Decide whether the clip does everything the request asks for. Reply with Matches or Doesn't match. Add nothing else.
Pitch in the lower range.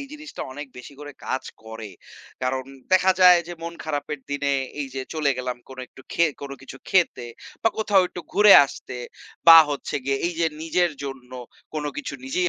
Doesn't match